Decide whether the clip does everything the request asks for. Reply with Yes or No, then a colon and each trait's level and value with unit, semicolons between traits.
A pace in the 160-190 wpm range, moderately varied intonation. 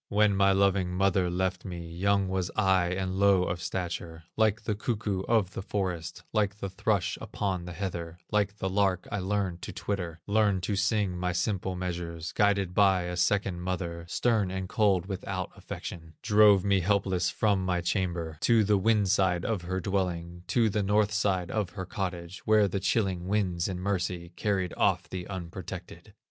No: average, 180 wpm; narrow, 2.3 semitones